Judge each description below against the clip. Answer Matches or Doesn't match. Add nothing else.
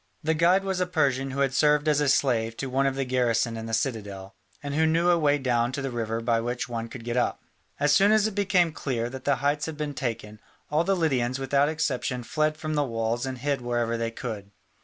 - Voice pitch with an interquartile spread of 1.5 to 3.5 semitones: Doesn't match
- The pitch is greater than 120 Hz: Matches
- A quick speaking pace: Matches